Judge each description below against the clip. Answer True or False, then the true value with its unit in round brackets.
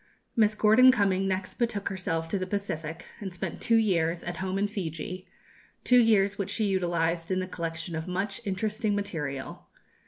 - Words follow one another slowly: False (175 wpm)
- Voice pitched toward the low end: False (190 Hz)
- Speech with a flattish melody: False (3.4 semitones)